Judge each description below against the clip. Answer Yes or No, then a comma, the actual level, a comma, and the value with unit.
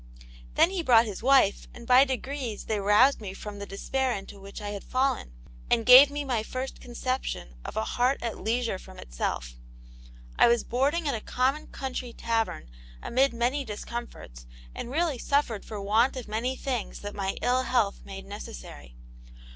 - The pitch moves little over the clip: No, average, 4.2 semitones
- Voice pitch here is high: Yes, high, 235 Hz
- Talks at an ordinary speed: Yes, average, 175 wpm